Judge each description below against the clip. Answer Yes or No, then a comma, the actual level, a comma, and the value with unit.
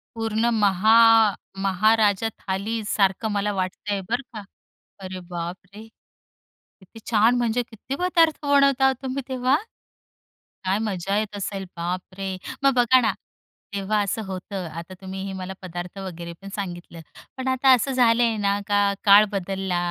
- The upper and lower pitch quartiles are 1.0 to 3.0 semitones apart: No, average, 3.4 semitones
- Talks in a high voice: Yes, high, 205 Hz